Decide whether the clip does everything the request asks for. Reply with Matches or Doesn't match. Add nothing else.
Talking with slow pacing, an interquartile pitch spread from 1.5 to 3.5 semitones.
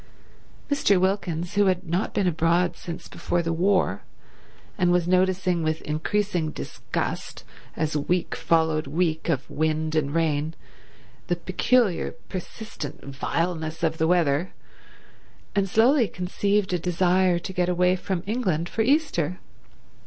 Matches